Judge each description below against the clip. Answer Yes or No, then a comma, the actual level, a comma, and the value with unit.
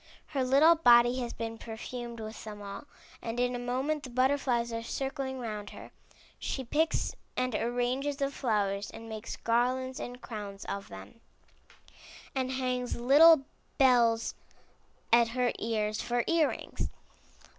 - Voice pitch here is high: Yes, high, 245 Hz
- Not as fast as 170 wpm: Yes, average, 145 wpm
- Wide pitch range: No, narrow, 2.6 semitones